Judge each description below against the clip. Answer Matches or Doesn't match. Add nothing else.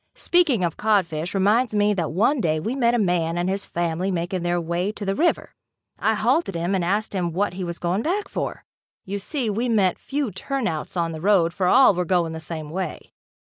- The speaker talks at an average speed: Doesn't match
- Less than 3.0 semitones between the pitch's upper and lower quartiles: Doesn't match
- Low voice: Doesn't match